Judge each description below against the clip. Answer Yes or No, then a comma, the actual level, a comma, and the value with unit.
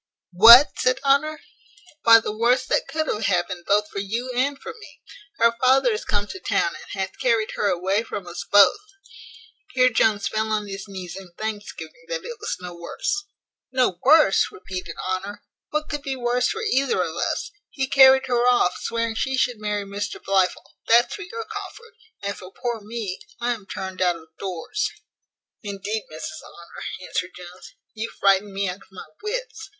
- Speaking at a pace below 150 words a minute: No, average, 185 wpm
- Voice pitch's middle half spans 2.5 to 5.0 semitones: No, wide, 5.4 semitones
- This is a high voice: Yes, high, 220 Hz